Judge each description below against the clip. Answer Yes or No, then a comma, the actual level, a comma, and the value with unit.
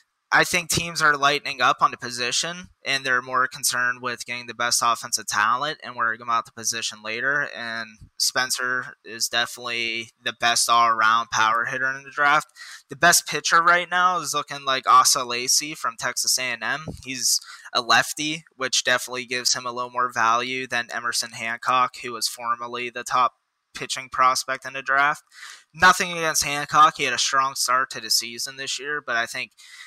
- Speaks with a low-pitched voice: Yes, low, 125 Hz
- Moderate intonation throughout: Yes, average, 3.3 semitones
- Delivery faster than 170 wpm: Yes, average, 185 wpm